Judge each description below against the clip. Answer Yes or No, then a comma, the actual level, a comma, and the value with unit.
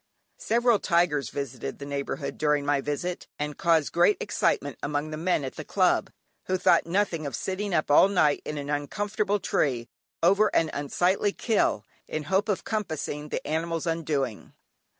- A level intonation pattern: No, average, 4.6 semitones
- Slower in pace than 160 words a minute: No, average, 165 wpm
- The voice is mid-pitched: Yes, medium, 160 Hz